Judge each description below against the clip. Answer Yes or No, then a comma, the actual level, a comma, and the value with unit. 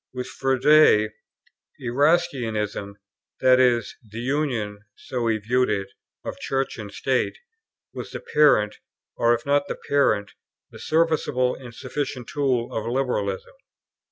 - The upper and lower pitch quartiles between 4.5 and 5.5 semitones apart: No, average, 4.1 semitones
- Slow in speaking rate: Yes, slow, 130 wpm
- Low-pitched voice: Yes, low, 125 Hz